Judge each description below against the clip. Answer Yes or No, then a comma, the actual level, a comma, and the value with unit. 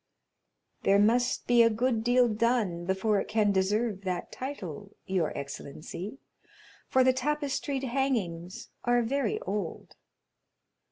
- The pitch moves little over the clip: No, average, 4.8 semitones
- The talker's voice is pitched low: No, high, 220 Hz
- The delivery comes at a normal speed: No, slow, 120 wpm